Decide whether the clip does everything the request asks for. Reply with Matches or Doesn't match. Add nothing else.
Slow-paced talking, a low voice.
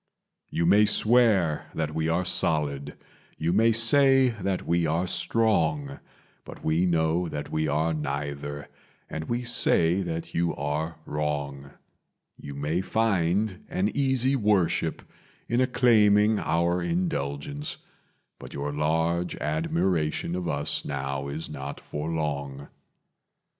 Matches